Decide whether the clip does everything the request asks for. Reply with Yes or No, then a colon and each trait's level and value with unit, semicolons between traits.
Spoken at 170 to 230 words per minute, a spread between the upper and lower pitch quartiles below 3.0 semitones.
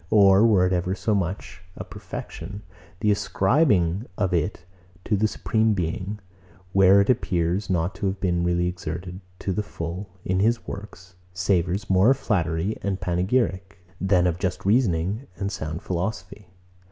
No: average, 155 wpm; narrow, 2.6 semitones